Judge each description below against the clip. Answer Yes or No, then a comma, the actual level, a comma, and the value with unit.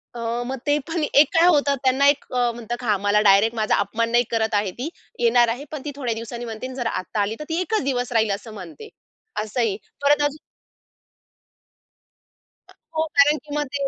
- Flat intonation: No, average, 4.5 semitones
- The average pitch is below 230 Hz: No, high, 245 Hz